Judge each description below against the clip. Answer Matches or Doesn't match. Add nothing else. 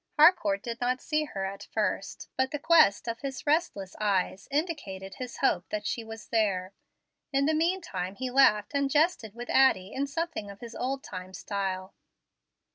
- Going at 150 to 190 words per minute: Matches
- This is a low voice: Doesn't match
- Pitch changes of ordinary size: Doesn't match